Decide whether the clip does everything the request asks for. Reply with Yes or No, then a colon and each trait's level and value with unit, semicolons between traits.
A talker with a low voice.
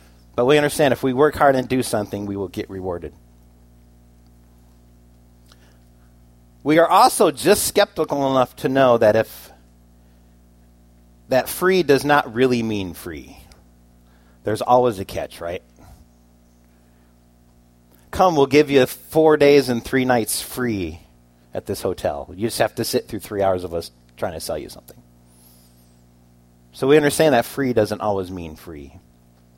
Yes: very low, 80 Hz